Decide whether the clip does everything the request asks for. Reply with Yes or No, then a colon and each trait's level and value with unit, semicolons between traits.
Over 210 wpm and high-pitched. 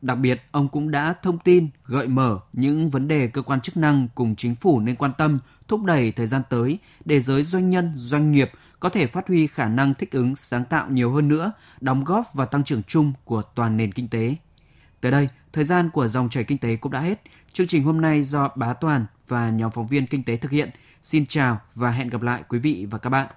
No: average, 245 wpm; low, 135 Hz